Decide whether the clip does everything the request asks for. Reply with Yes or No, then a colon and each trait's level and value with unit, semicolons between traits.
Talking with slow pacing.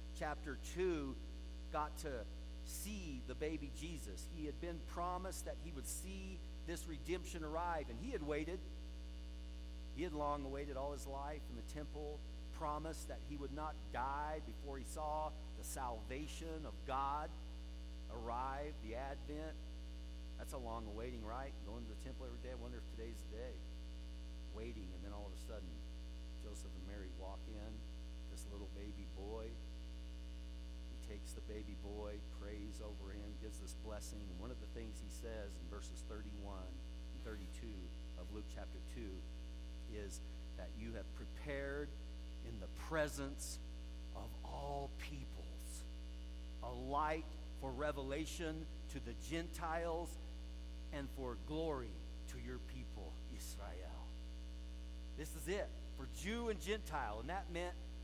No: average, 145 wpm